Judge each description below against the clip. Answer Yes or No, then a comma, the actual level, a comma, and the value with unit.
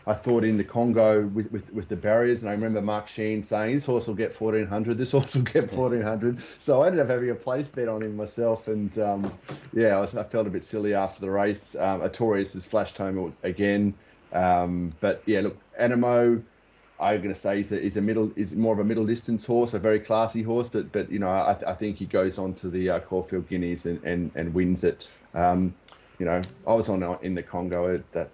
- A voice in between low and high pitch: No, low, 105 Hz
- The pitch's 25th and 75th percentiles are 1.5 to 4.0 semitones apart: Yes, average, 3.4 semitones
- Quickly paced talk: Yes, fast, 235 wpm